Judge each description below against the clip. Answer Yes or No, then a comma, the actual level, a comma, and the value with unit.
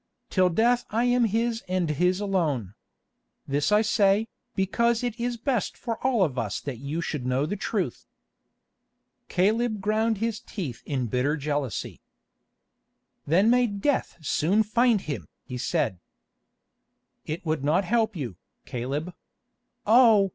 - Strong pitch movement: Yes, wide, 7.5 semitones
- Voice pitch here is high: Yes, high, 195 Hz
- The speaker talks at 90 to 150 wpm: Yes, average, 140 wpm